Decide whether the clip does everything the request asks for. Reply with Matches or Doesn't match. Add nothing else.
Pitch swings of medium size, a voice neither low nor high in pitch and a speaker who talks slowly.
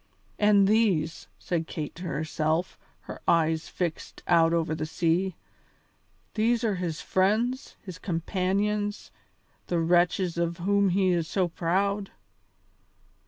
Matches